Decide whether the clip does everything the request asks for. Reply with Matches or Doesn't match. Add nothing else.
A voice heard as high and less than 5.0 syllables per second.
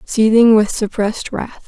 Matches